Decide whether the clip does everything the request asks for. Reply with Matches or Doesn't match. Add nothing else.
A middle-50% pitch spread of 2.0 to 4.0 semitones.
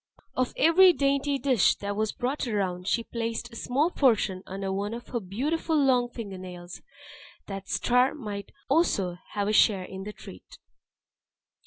Doesn't match